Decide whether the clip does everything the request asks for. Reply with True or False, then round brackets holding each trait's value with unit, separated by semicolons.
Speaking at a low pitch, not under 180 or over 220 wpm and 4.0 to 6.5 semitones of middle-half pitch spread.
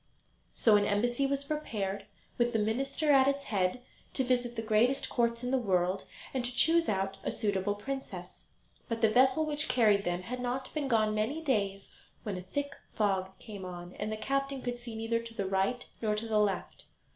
False (225 Hz; 200 wpm; 4.4 semitones)